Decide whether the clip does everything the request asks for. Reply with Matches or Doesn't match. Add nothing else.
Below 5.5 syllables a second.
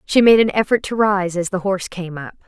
Doesn't match